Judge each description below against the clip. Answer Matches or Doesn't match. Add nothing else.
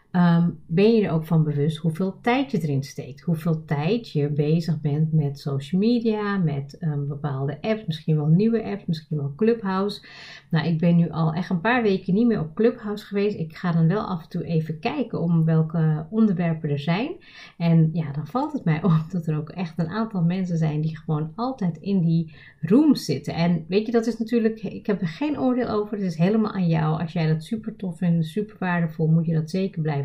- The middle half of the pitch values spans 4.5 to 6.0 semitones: Matches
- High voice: Doesn't match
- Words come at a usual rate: Doesn't match